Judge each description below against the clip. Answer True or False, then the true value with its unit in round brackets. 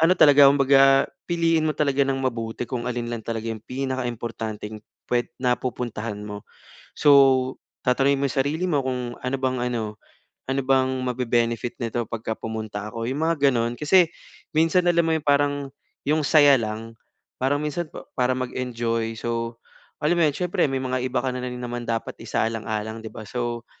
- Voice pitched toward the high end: False (125 Hz)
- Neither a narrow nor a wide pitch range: True (3.3 semitones)